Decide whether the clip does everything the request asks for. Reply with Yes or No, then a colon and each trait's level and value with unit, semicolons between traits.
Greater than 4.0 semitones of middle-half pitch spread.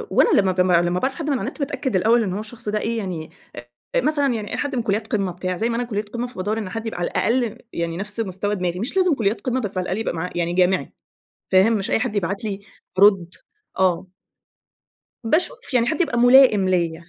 Yes: average, 4.6 semitones